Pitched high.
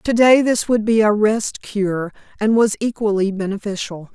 Yes: high, 210 Hz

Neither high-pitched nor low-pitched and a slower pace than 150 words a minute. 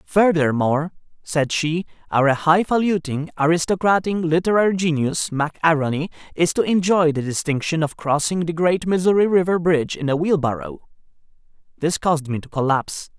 Yes: medium, 165 Hz; slow, 135 wpm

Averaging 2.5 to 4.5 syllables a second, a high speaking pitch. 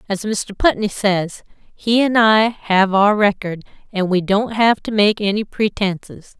Yes: 4.0 syllables/s; high, 205 Hz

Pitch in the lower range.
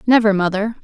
No: high, 210 Hz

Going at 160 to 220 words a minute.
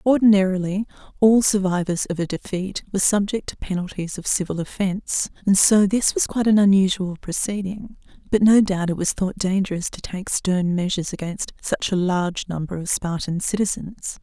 Yes: average, 170 wpm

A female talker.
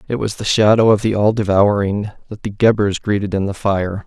No: male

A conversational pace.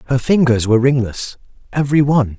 Yes: average, 150 wpm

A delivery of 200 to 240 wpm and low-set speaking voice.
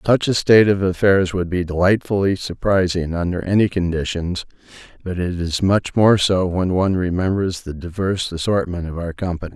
No: average, 170 wpm; very low, 90 Hz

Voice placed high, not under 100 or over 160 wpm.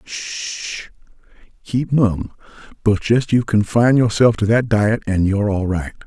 No: low, 110 Hz; average, 140 wpm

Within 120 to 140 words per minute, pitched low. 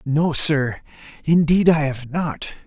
No: slow, 135 wpm; medium, 150 Hz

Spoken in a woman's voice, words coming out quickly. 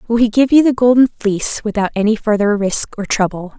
Yes: female; fast, 220 wpm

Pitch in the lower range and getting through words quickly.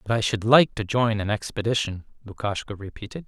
No: low, 110 Hz; average, 185 wpm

